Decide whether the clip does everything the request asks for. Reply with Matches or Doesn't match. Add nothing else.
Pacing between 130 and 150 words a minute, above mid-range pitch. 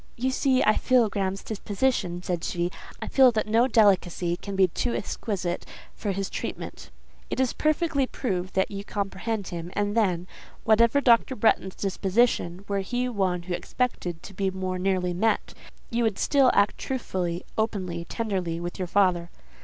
Doesn't match